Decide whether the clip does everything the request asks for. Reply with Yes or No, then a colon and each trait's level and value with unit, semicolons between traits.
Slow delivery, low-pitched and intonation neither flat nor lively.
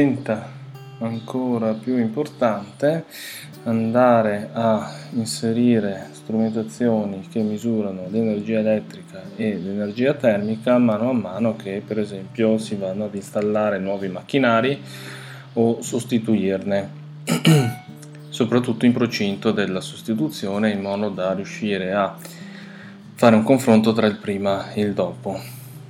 Yes: slow, 110 wpm; low, 110 Hz; average, 3.2 semitones